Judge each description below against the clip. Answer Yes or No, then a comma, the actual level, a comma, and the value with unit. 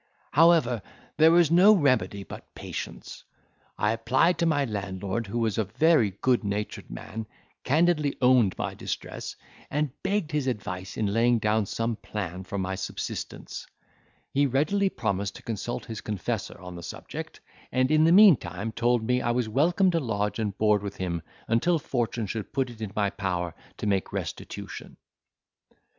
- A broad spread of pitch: Yes, wide, 6.1 semitones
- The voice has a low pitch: Yes, low, 115 Hz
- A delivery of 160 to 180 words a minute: Yes, average, 165 wpm